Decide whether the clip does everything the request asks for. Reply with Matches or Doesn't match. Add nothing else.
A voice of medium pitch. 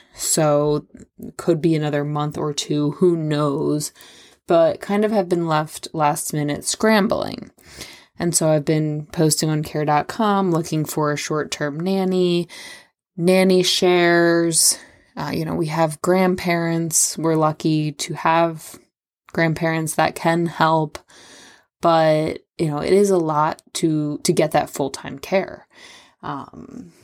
Matches